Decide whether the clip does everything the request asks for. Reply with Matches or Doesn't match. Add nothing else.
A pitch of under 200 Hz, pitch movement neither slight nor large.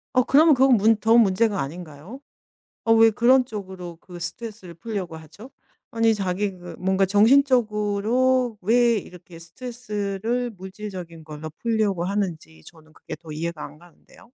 Doesn't match